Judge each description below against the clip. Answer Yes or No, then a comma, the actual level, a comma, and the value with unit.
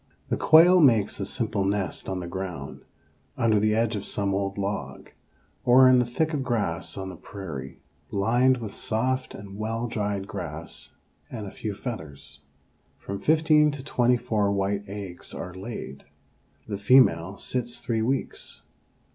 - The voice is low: Yes, low, 105 Hz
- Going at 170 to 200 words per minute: No, average, 155 wpm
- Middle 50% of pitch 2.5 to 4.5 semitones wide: Yes, average, 3.9 semitones